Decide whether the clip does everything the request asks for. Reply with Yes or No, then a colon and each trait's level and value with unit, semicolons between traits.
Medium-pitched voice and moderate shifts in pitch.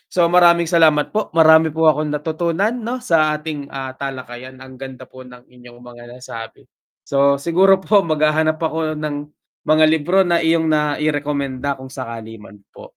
Yes: medium, 150 Hz; average, 3.7 semitones